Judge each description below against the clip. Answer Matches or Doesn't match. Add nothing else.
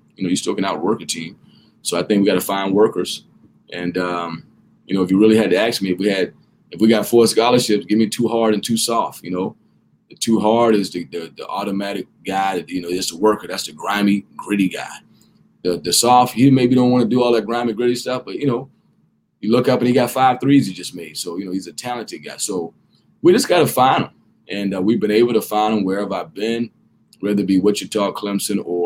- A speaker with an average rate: Doesn't match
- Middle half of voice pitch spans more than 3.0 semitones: Matches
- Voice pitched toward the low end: Matches